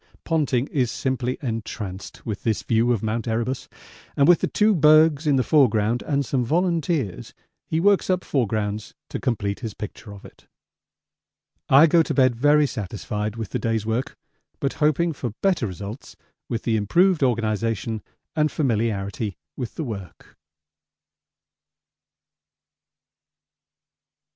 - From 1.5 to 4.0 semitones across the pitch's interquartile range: No, wide, 5.5 semitones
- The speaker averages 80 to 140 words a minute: Yes, slow, 135 wpm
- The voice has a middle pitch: No, low, 120 Hz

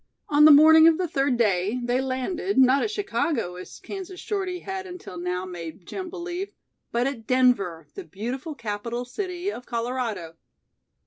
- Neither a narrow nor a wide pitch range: No, wide, 8.3 semitones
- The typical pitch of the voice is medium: No, very high, 260 Hz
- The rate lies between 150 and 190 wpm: Yes, average, 165 wpm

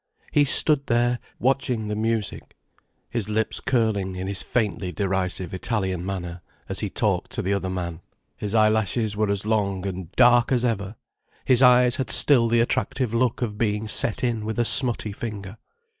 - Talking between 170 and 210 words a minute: Yes, average, 175 wpm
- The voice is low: Yes, low, 110 Hz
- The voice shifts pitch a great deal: No, average, 3.6 semitones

